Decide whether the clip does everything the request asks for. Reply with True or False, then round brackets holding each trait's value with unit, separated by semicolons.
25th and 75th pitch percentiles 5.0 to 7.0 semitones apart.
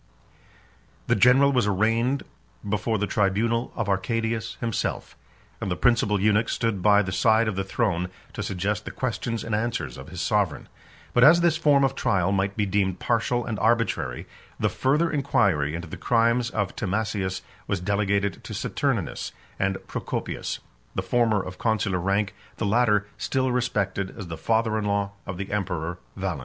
False (3.3 semitones)